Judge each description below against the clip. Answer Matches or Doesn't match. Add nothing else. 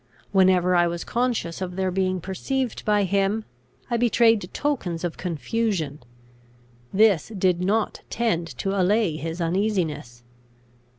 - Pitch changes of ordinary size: Matches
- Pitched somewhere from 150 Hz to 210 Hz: Matches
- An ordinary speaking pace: Doesn't match